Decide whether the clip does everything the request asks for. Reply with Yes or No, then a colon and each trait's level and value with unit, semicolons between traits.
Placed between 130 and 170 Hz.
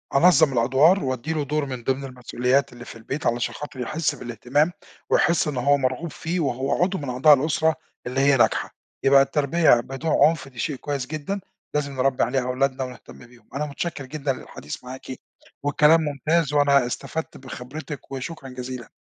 Yes: low, 135 Hz